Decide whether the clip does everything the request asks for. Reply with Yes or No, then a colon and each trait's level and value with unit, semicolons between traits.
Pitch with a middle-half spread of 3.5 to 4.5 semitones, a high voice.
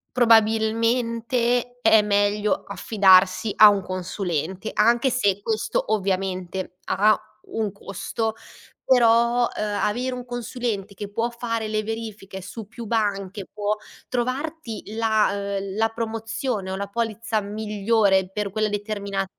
No: narrow, 2.5 semitones; high, 215 Hz